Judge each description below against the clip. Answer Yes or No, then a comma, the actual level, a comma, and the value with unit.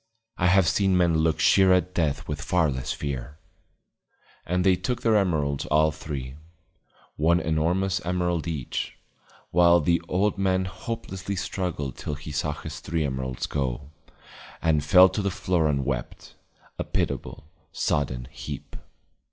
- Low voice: Yes, very low, 80 Hz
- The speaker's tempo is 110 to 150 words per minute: Yes, average, 145 wpm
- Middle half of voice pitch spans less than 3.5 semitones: No, average, 4.0 semitones